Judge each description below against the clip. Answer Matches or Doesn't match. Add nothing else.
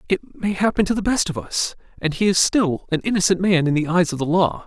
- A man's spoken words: Matches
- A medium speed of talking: Doesn't match